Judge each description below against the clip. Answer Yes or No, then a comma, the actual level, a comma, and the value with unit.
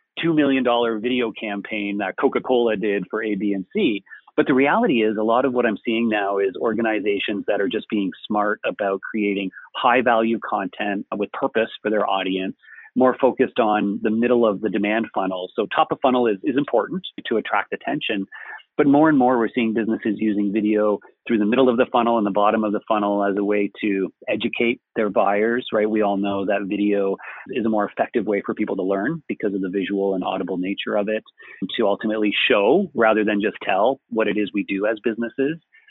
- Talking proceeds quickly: Yes, fast, 210 wpm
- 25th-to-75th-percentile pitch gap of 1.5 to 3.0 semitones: Yes, average, 2.7 semitones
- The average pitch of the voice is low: Yes, low, 110 Hz